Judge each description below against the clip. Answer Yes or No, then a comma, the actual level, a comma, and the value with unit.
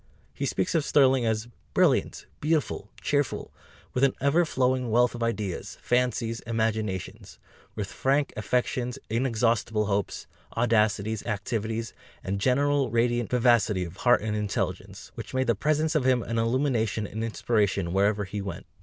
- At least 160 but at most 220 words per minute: No, average, 145 wpm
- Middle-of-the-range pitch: No, low, 115 Hz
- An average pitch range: Yes, average, 3.3 semitones